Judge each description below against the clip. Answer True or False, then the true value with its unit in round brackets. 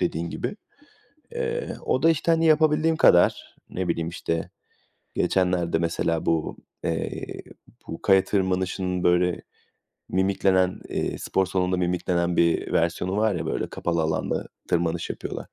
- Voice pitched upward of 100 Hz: False (90 Hz)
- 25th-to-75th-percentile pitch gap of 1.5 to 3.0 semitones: True (2.4 semitones)